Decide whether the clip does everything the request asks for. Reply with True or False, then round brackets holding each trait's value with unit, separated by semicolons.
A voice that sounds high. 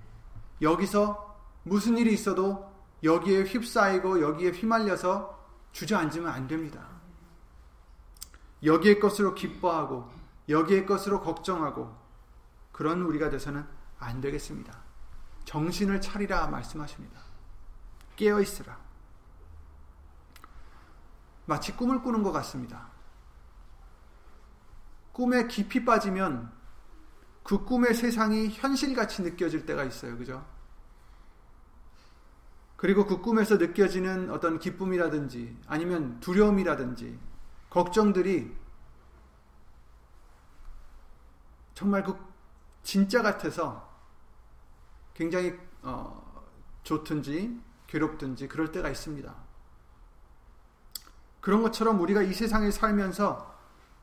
False (155 Hz)